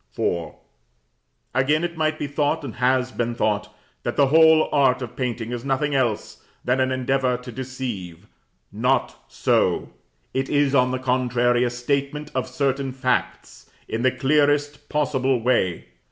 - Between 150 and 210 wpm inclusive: Yes, average, 155 wpm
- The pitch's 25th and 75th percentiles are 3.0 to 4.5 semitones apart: No, narrow, 2.5 semitones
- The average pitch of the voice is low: Yes, low, 130 Hz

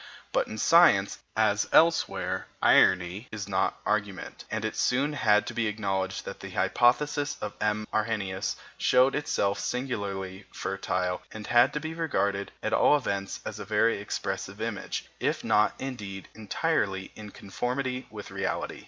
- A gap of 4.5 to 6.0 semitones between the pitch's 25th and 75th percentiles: No, average, 4.1 semitones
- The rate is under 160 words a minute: Yes, average, 150 wpm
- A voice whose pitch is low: Yes, low, 105 Hz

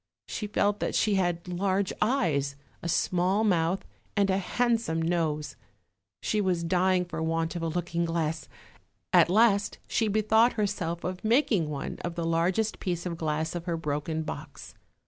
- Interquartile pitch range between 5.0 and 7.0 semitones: No, average, 3.6 semitones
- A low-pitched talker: No, medium, 175 Hz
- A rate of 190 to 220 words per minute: No, average, 165 wpm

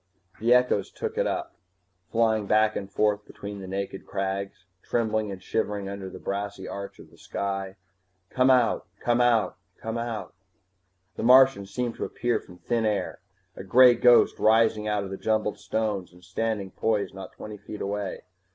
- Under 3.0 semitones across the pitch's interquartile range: Yes, narrow, 2.6 semitones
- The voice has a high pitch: No, low, 105 Hz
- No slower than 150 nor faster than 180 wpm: Yes, average, 170 wpm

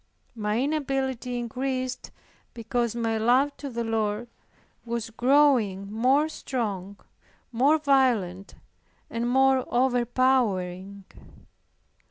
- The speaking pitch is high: Yes, high, 240 Hz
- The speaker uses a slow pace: Yes, slow, 90 wpm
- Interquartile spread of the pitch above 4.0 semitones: No, average, 3.3 semitones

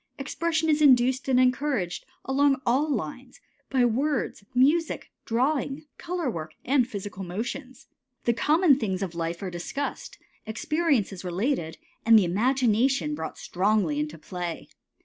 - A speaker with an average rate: No, slow, 130 wpm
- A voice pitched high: Yes, very high, 250 Hz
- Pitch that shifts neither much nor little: No, wide, 6.7 semitones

